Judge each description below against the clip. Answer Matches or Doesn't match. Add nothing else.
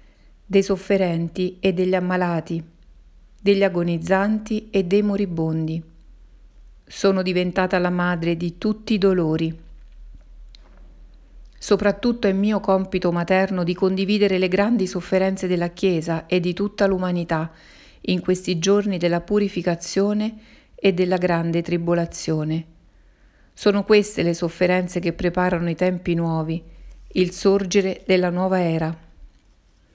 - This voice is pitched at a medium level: Matches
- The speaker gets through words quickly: Doesn't match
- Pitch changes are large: Doesn't match